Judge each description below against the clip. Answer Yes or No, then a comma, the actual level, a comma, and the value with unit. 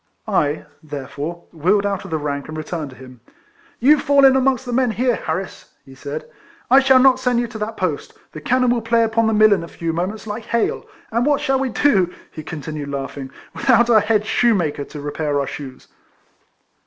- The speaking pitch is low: No, high, 205 Hz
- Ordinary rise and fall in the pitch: No, wide, 8.2 semitones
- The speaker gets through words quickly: Yes, fast, 215 wpm